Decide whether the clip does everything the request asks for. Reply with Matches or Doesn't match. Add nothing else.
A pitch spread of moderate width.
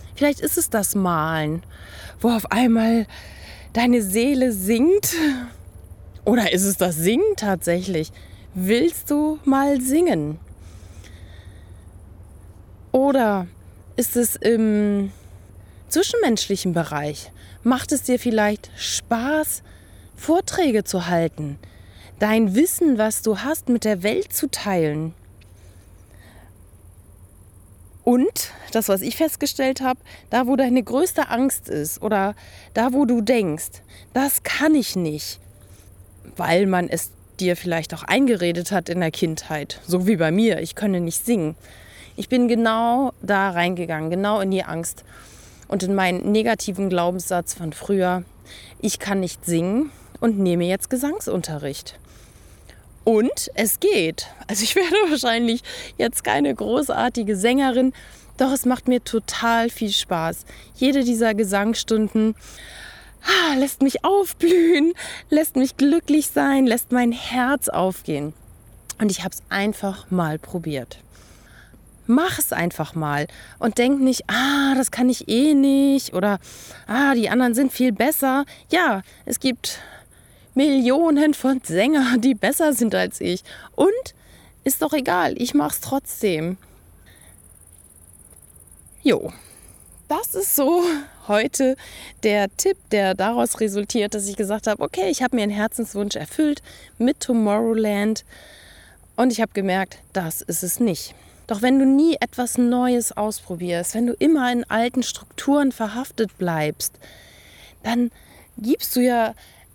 Doesn't match